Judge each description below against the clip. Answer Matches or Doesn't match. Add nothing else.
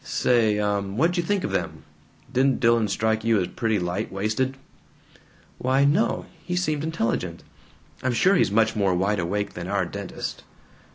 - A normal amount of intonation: Matches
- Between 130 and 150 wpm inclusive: Doesn't match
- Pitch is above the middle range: Doesn't match